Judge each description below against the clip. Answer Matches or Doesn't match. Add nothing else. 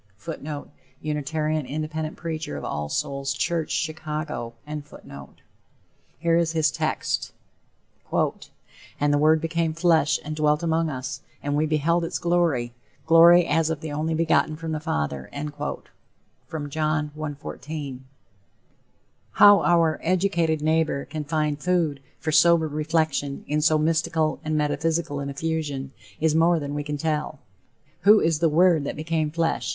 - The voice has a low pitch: Doesn't match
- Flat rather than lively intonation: Matches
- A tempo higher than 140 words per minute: Doesn't match